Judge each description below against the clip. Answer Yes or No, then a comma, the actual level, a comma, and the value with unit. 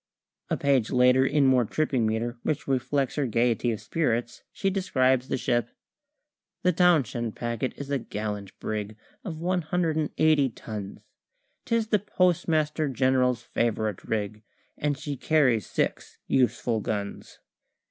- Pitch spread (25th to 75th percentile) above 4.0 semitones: Yes, average, 4.9 semitones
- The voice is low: Yes, low, 130 Hz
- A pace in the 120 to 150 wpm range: Yes, average, 140 wpm